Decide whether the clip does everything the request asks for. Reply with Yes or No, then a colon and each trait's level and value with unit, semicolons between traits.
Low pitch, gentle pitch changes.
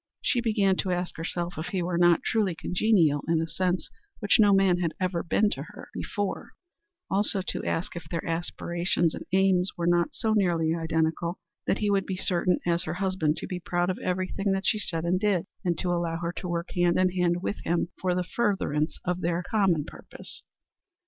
No: medium, 180 Hz; narrow, 2.1 semitones